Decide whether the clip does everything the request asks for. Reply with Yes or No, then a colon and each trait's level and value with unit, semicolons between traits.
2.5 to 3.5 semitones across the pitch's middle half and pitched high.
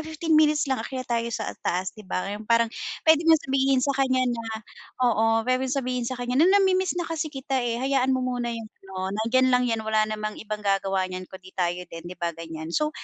No: average, 4.2 semitones; high, 235 Hz